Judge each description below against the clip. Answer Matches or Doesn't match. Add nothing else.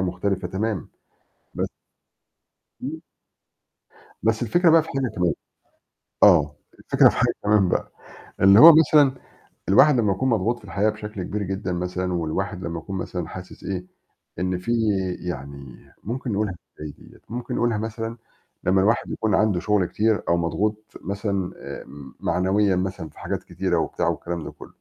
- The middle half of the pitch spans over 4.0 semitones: Doesn't match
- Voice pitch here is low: Matches